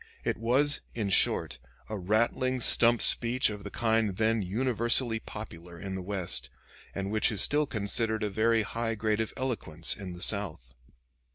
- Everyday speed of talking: Yes, average, 165 wpm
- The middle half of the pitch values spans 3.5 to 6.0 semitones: No, average, 3.0 semitones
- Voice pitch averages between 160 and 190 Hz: No, low, 110 Hz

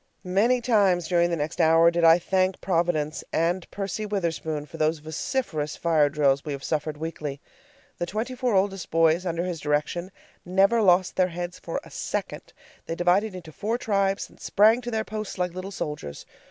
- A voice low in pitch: No, medium, 175 Hz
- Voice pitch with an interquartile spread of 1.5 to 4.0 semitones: Yes, average, 3.7 semitones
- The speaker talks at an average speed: Yes, average, 180 wpm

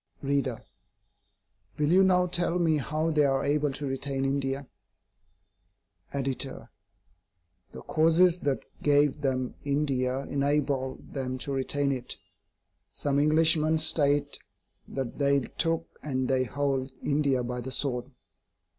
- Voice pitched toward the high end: No, medium, 140 Hz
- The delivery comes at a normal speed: No, slow, 120 wpm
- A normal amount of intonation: No, narrow, 2.2 semitones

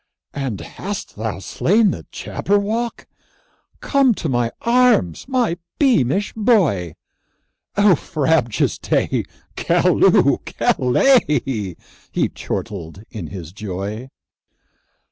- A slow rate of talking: Yes, slow, 90 wpm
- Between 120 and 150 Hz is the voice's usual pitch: Yes, medium, 140 Hz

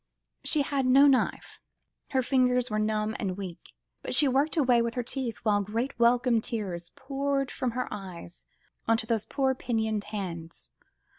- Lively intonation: No, average, 3.8 semitones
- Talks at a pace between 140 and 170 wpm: Yes, average, 160 wpm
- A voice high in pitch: Yes, high, 235 Hz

